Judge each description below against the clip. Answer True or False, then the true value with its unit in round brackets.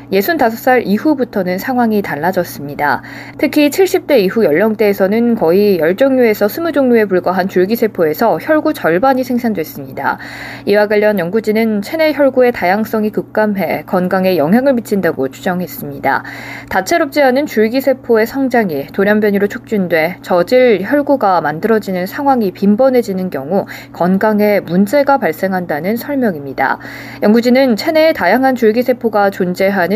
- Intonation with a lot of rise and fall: True (5.7 semitones)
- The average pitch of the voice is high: True (210 Hz)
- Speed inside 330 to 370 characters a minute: True (335 characters per minute)